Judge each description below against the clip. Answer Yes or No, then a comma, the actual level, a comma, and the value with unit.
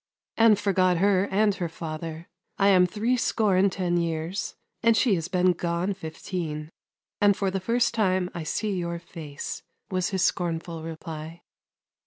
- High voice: No, medium, 180 Hz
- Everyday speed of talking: Yes, average, 165 wpm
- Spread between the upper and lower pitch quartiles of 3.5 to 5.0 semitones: No, average, 3.1 semitones